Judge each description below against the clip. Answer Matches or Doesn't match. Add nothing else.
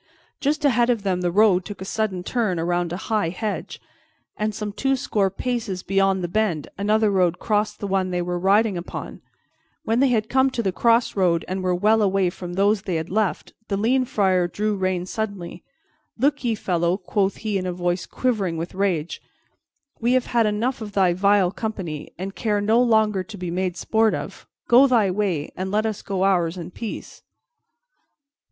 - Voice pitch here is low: Doesn't match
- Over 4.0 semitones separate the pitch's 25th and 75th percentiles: Doesn't match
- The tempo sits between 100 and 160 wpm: Doesn't match